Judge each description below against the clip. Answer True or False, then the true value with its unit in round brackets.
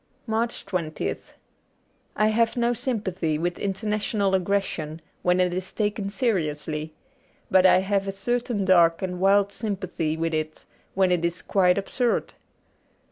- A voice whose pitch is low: False (190 Hz)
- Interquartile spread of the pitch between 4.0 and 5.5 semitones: False (3.2 semitones)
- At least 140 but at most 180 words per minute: True (145 wpm)